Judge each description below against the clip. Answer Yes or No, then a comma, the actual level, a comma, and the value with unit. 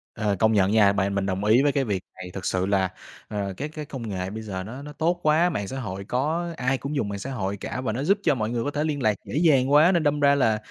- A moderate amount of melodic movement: No, wide, 6.4 semitones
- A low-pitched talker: Yes, low, 120 Hz